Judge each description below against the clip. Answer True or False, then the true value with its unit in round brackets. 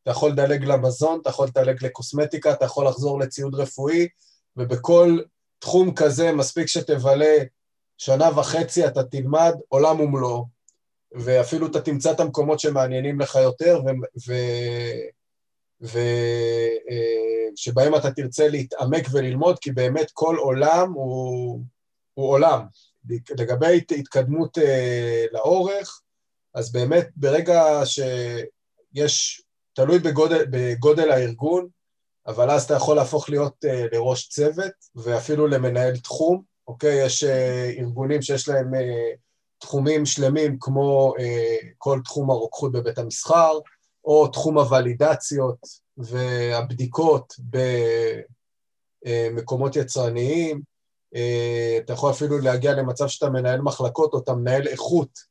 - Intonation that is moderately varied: True (3.4 semitones)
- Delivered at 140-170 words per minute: False (115 wpm)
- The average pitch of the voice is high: False (135 Hz)